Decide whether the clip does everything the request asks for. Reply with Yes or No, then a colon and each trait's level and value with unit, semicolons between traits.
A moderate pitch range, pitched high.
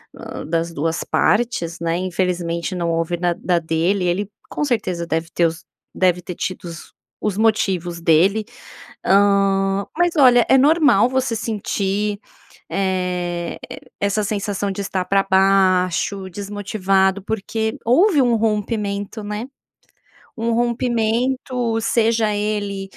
Yes: average, 3.6 semitones; high, 200 Hz